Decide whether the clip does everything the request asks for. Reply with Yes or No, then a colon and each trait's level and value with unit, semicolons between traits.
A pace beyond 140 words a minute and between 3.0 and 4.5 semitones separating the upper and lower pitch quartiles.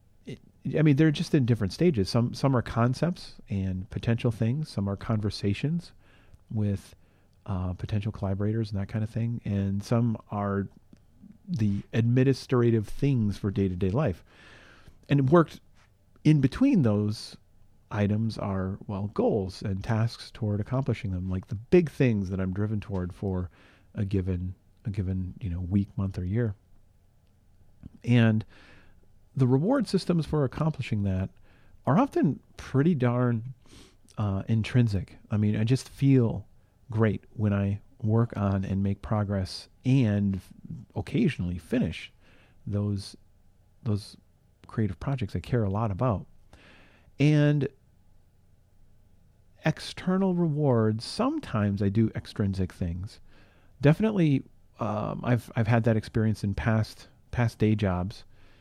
No: slow, 135 wpm; average, 3.9 semitones